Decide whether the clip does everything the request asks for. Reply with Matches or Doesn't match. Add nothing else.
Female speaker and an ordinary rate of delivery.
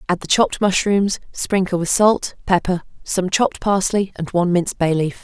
Matches